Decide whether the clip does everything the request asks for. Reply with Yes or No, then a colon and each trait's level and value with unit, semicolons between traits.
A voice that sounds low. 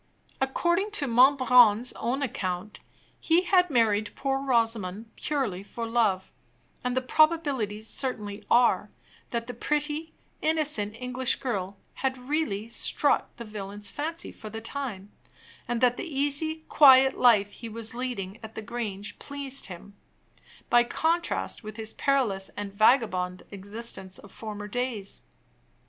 No: high, 235 Hz